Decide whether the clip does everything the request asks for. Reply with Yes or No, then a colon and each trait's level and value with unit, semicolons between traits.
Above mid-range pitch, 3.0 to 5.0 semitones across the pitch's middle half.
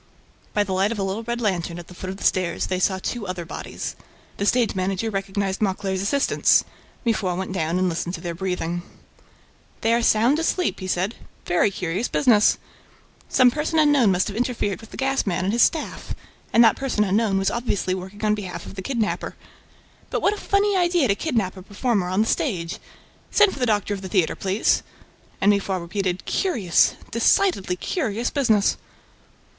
Yes: high, 200 Hz; average, 4.2 semitones